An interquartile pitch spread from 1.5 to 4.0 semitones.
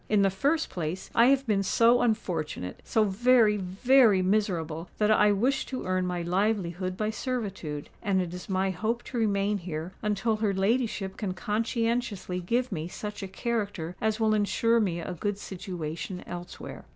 Yes: average, 3.6 semitones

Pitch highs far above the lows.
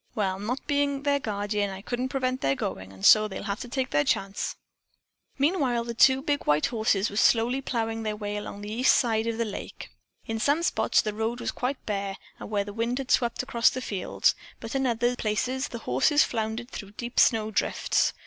No: average, 3.7 semitones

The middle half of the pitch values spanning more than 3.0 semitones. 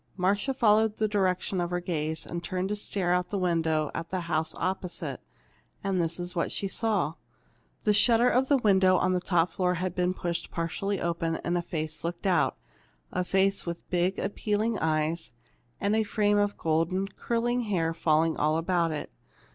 Yes: average, 3.4 semitones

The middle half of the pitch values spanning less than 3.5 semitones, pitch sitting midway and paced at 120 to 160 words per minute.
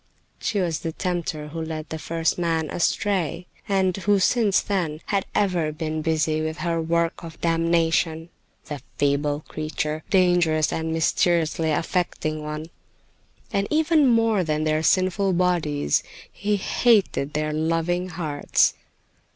Yes: average, 2.8 semitones; medium, 165 Hz; slow, 135 wpm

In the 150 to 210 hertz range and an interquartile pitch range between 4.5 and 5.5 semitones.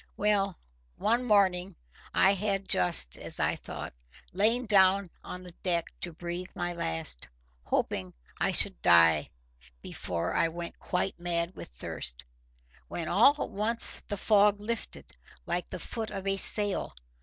No: medium, 185 Hz; average, 3.4 semitones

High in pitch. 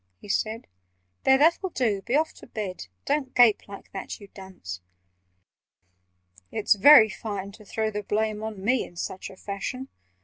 Yes: high, 215 Hz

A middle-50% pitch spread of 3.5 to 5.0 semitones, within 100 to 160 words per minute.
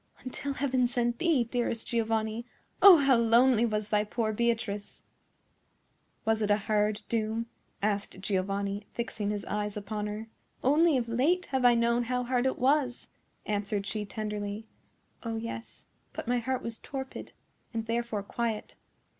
No: average, 2.7 semitones; average, 150 wpm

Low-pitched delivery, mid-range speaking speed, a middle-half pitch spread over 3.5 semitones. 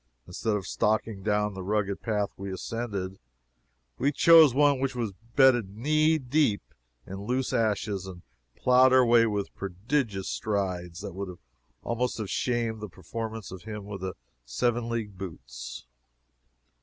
Yes: low, 105 Hz; average, 145 wpm; average, 4.0 semitones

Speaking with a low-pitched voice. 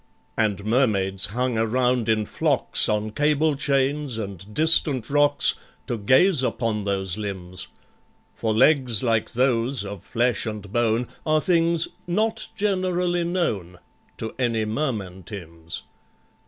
Yes: low, 120 Hz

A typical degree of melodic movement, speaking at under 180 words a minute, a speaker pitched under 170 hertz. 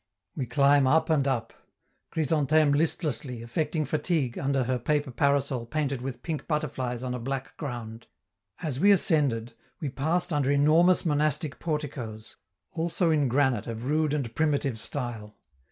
Yes: average, 3.7 semitones; average, 145 wpm; medium, 140 Hz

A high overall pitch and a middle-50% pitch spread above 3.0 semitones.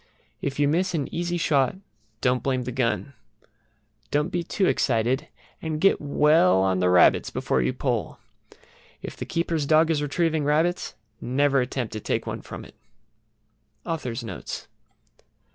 No: medium, 145 Hz; average, 4.4 semitones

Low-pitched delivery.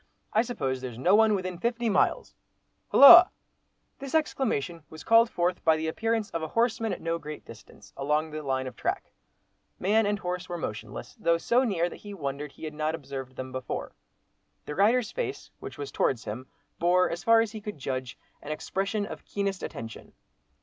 No: medium, 175 Hz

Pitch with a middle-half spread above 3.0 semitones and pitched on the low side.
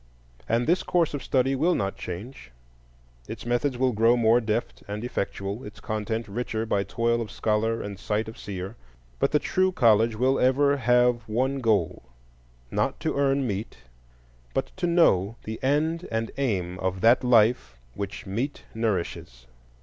Yes: average, 4.3 semitones; low, 115 Hz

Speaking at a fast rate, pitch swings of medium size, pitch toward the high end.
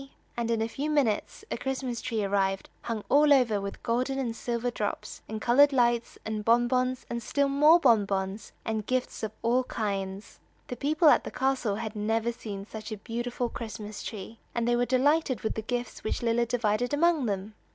No: average, 190 wpm; average, 3.0 semitones; high, 235 Hz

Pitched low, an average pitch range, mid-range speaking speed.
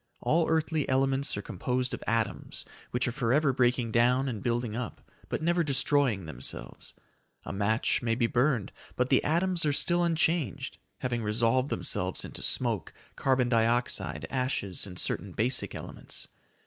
Yes: low, 125 Hz; average, 3.5 semitones; average, 150 wpm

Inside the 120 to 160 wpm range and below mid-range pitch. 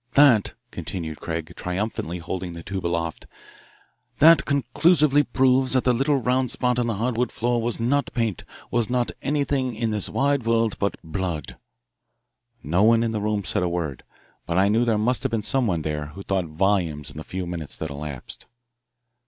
No: average, 180 wpm; low, 110 Hz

